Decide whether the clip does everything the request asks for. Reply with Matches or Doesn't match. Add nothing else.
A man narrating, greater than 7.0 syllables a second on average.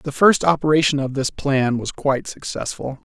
Doesn't match